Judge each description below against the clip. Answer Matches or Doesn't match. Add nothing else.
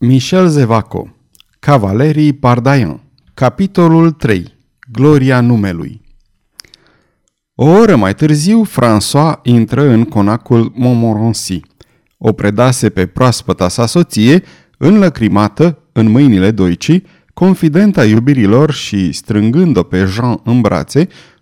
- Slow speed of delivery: Matches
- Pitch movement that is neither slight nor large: Doesn't match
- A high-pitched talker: Doesn't match